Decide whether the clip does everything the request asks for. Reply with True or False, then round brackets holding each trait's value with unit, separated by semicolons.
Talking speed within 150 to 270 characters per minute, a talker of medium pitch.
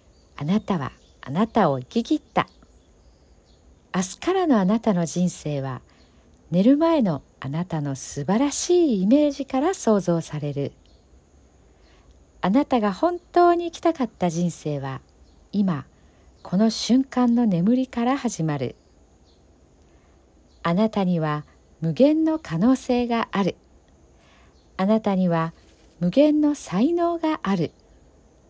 True (230 characters per minute; 175 Hz)